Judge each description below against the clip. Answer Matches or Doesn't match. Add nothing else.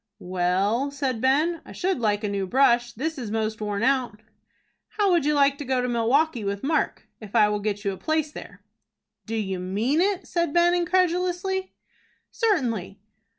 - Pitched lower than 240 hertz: Doesn't match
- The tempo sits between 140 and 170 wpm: Doesn't match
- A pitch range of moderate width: Doesn't match